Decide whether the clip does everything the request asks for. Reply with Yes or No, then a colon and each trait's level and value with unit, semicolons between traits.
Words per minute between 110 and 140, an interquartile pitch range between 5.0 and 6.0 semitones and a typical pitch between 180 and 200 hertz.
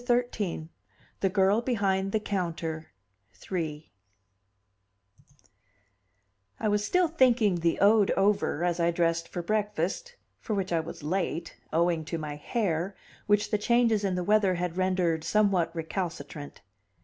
No: slow, 135 wpm; average, 3.9 semitones; medium, 185 Hz